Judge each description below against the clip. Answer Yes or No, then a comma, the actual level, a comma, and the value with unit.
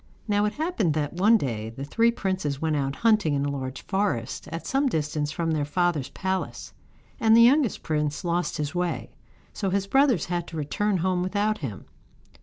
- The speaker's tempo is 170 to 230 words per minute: Yes, average, 190 wpm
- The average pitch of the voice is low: No, medium, 175 Hz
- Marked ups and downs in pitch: Yes, wide, 5.9 semitones